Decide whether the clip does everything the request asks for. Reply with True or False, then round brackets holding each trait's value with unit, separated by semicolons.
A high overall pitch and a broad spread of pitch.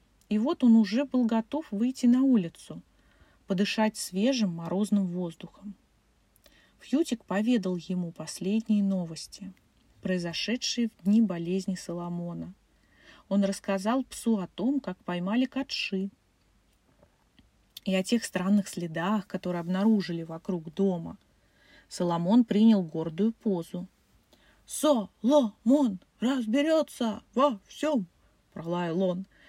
False (200 Hz; 4.5 semitones)